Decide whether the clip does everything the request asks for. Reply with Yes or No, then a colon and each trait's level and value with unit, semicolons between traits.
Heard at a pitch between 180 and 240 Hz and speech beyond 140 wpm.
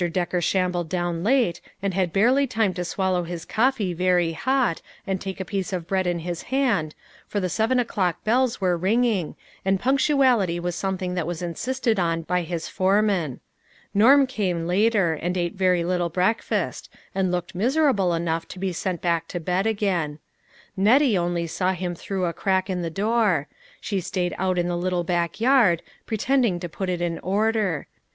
Yes: medium, 185 Hz; average, 180 wpm